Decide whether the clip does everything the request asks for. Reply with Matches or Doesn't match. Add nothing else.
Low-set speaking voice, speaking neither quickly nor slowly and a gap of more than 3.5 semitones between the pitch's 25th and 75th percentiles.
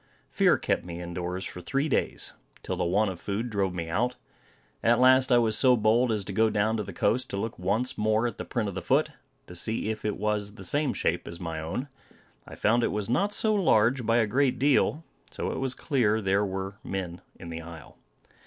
Doesn't match